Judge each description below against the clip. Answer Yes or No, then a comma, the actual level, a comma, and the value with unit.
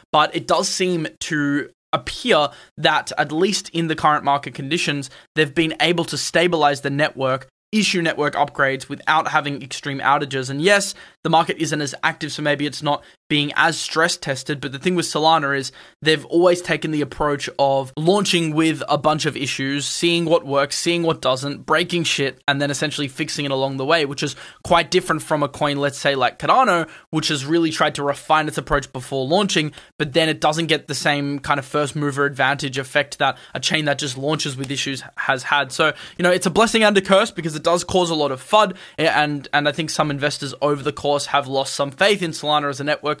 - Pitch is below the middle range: No, medium, 150 Hz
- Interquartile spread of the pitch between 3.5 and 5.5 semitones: No, narrow, 2.5 semitones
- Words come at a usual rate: No, fast, 215 wpm